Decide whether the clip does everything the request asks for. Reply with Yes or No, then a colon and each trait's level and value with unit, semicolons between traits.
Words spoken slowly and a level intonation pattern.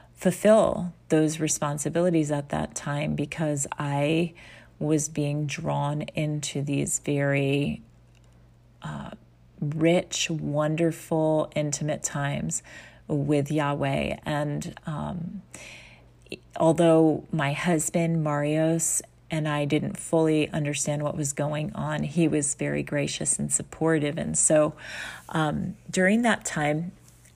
Yes: slow, 105 wpm; narrow, 2.2 semitones